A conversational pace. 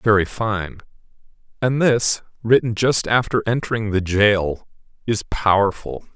No: slow, 125 wpm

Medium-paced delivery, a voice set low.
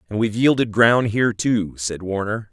Yes: average, 190 wpm; low, 105 Hz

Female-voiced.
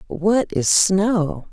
Yes: female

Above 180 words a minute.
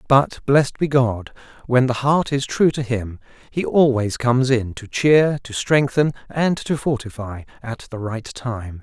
No: average, 175 wpm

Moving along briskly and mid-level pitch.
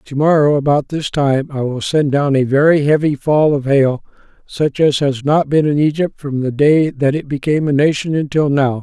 Yes: fast, 220 wpm; medium, 145 Hz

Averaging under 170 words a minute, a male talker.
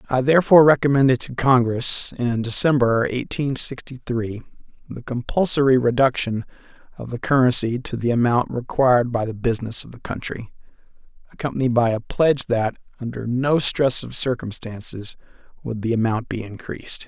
Yes: average, 145 wpm; male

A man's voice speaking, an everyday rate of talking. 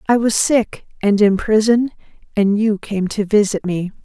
No: female; average, 180 wpm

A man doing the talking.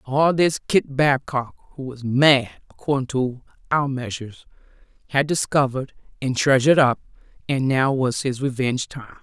No: female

